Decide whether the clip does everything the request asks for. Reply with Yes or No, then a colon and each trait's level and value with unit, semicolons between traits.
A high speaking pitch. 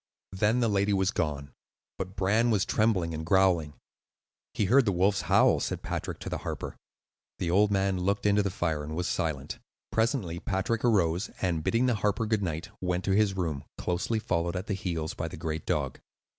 No: very low, 95 Hz